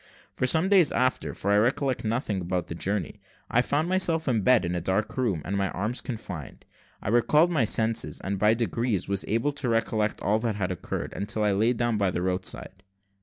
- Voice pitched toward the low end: Yes, low, 110 Hz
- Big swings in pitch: No, average, 4.3 semitones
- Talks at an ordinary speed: No, fast, 210 wpm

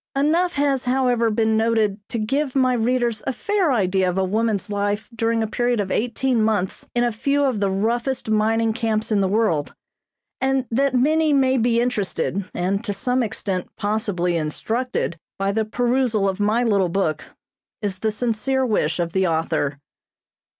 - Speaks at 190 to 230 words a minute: No, average, 170 wpm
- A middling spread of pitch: Yes, average, 4.0 semitones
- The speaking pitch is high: Yes, high, 225 Hz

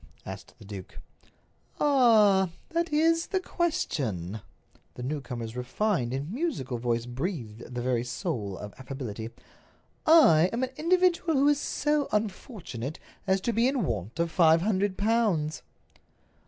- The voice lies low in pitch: No, medium, 170 Hz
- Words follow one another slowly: Yes, slow, 130 wpm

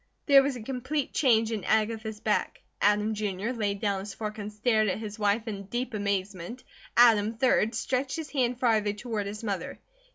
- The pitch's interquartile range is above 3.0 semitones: No, average, 2.7 semitones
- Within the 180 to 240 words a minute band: Yes, average, 185 wpm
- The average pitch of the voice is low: No, high, 220 Hz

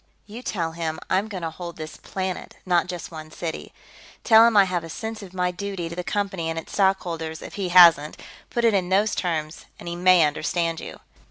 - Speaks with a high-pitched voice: No, medium, 180 Hz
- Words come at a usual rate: No, fast, 220 wpm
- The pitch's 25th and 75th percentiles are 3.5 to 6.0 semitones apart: No, average, 3.0 semitones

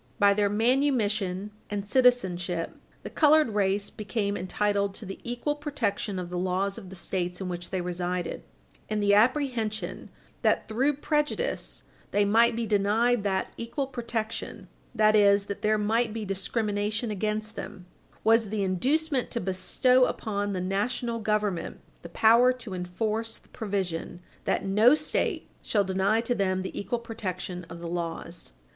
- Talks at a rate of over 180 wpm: No, average, 155 wpm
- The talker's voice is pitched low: No, high, 210 Hz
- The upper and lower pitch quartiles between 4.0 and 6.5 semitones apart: No, average, 3.5 semitones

